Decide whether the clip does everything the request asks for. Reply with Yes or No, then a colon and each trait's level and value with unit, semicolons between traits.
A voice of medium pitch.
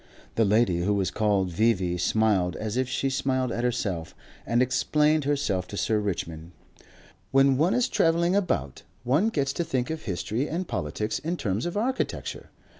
No: low, 120 Hz